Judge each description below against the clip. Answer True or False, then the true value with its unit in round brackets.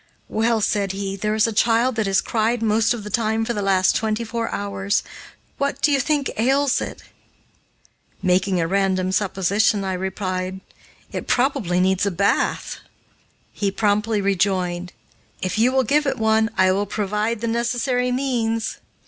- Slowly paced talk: False (165 wpm)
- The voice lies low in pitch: False (210 Hz)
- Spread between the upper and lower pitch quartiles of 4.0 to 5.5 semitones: False (3.2 semitones)